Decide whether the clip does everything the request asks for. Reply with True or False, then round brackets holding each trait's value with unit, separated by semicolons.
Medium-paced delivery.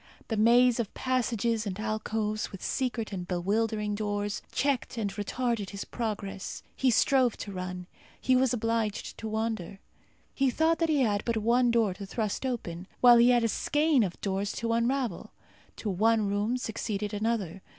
True (170 wpm)